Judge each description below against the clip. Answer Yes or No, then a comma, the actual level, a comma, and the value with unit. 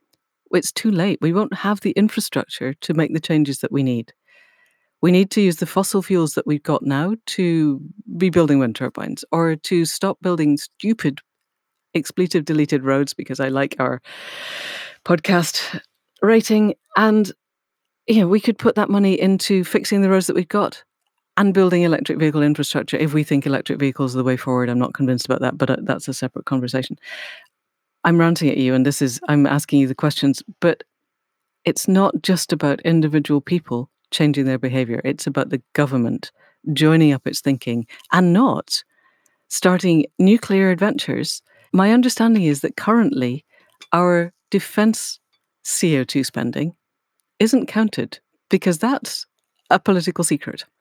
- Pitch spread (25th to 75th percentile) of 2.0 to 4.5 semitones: No, wide, 5.6 semitones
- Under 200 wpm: Yes, average, 160 wpm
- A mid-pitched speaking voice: Yes, medium, 165 Hz